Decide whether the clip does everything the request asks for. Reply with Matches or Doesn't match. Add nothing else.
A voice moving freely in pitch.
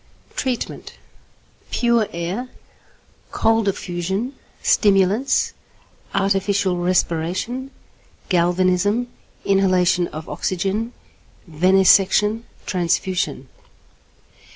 Doesn't match